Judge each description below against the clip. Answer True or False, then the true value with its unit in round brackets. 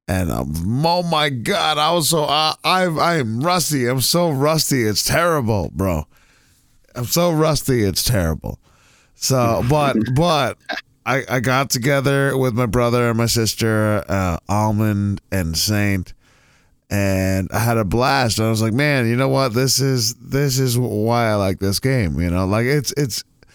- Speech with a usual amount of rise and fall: True (5.0 semitones)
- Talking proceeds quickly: False (170 wpm)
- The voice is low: True (120 Hz)